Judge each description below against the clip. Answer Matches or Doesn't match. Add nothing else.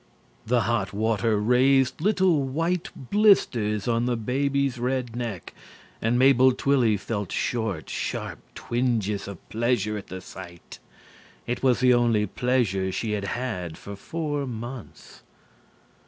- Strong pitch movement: Doesn't match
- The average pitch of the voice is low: Matches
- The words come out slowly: Matches